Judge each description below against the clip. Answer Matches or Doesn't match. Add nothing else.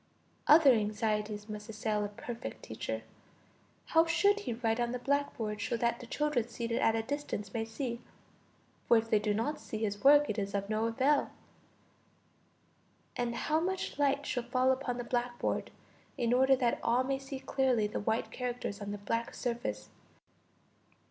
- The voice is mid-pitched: Doesn't match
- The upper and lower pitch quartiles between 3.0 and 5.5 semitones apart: Matches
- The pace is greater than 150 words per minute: Matches